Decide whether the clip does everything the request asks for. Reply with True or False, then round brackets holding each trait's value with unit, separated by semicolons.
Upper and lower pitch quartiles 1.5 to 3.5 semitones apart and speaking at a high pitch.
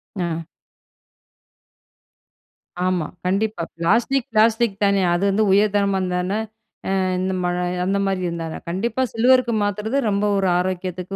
True (3.1 semitones; 195 Hz)